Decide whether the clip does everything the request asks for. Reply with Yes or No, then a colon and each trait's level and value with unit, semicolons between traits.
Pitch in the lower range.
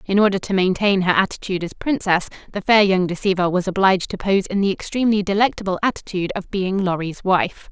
No: high, 190 Hz